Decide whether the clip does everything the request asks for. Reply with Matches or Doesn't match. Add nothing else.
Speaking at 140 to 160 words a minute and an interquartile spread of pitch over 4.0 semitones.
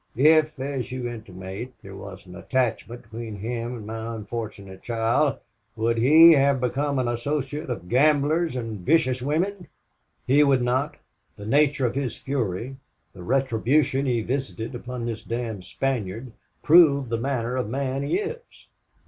Doesn't match